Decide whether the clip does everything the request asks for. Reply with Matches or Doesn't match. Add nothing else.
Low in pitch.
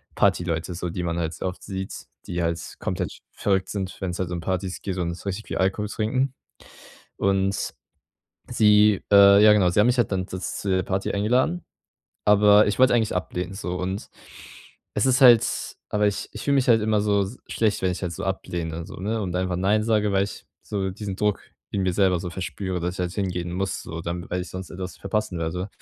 Matches